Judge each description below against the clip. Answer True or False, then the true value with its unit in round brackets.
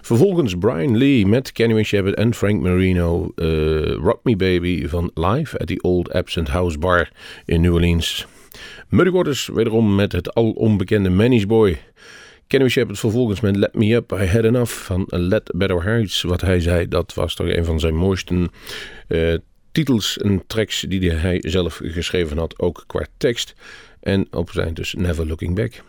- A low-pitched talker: True (95 Hz)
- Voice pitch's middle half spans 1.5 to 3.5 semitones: False (4.1 semitones)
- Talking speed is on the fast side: False (175 wpm)